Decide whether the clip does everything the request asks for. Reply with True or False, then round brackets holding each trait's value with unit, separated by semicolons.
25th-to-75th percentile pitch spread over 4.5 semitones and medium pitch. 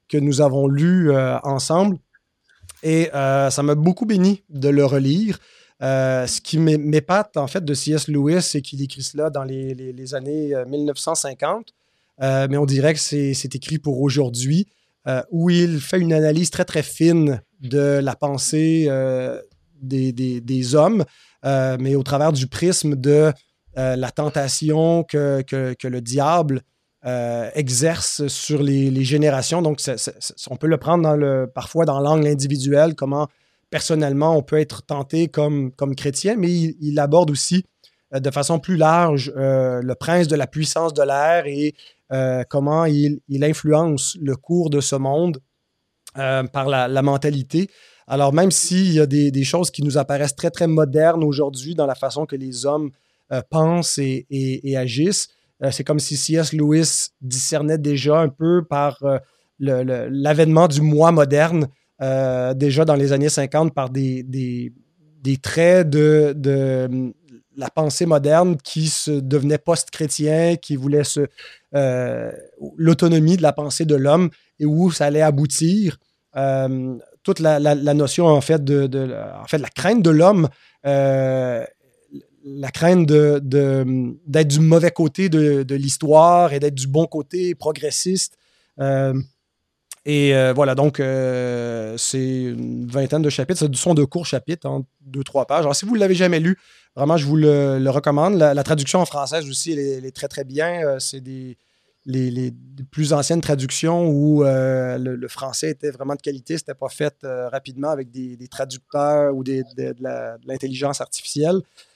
False (2.8 semitones; 145 Hz)